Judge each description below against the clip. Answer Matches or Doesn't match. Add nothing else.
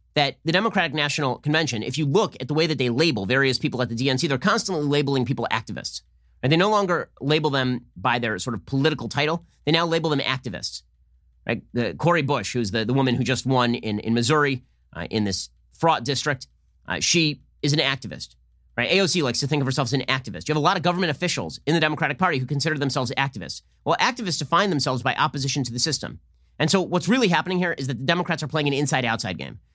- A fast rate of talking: Matches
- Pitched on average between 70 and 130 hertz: Doesn't match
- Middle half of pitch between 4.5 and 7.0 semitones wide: Matches